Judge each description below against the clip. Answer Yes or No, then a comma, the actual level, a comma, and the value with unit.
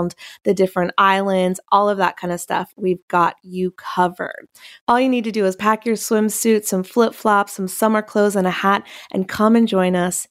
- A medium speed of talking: No, fast, 210 wpm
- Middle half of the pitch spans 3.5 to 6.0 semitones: No, average, 2.9 semitones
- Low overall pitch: No, high, 200 Hz